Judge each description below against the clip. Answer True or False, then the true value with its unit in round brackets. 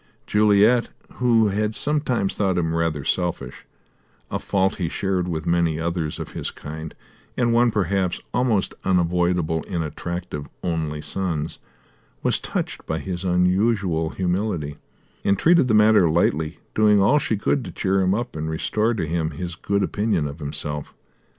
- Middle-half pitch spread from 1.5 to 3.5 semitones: False (4.5 semitones)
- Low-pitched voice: True (90 Hz)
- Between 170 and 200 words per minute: False (155 wpm)